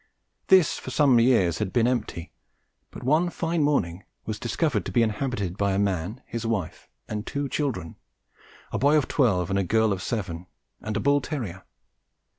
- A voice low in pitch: Yes, low, 115 Hz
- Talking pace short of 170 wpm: No, average, 180 wpm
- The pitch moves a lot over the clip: Yes, wide, 6.3 semitones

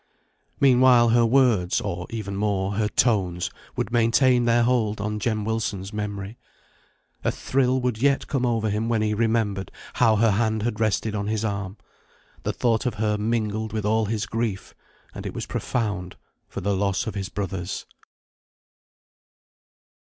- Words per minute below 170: Yes, average, 160 wpm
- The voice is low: Yes, low, 110 Hz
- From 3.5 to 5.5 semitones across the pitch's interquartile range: No, narrow, 2.4 semitones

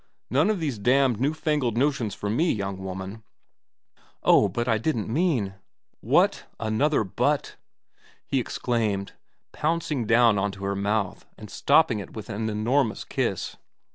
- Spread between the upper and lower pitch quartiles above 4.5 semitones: Yes, average, 5.3 semitones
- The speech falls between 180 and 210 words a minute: No, average, 160 wpm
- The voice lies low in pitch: Yes, low, 115 Hz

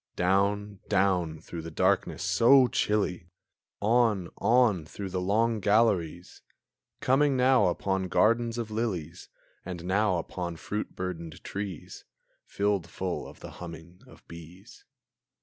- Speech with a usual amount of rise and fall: Yes, average, 3.9 semitones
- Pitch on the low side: Yes, very low, 95 Hz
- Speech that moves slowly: Yes, slow, 125 wpm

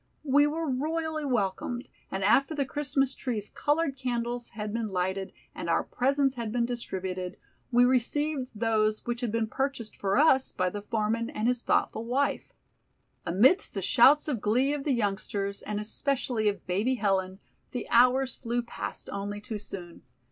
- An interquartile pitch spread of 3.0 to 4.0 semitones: No, average, 4.5 semitones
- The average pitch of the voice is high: Yes, high, 235 Hz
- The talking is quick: No, average, 165 wpm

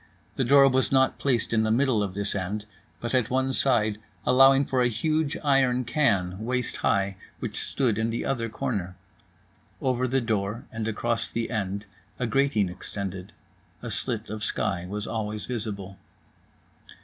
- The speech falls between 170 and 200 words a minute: No, average, 160 wpm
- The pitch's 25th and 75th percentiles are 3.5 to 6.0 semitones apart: Yes, average, 4.0 semitones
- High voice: No, low, 115 Hz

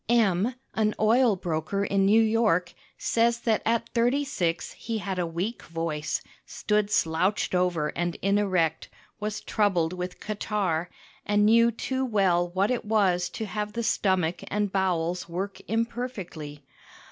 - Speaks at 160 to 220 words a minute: No, average, 145 wpm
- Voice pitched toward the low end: No, high, 200 Hz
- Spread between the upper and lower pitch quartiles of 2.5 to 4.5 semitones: Yes, average, 4.0 semitones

